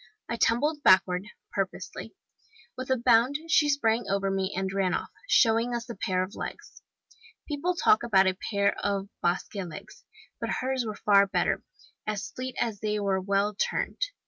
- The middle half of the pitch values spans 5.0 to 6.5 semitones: No, average, 4.3 semitones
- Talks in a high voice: Yes, high, 210 Hz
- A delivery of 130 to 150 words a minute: No, average, 170 wpm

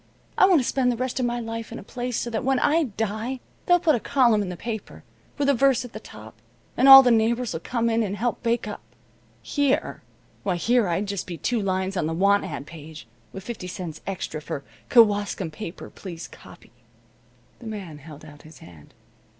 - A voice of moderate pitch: No, high, 220 Hz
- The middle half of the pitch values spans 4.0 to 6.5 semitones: Yes, wide, 5.5 semitones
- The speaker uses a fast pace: Yes, fast, 210 wpm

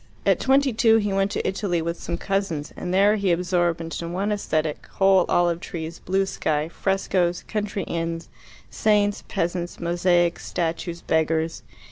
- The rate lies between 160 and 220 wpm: No, average, 150 wpm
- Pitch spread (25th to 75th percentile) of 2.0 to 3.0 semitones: Yes, average, 2.7 semitones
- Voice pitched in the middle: Yes, medium, 175 Hz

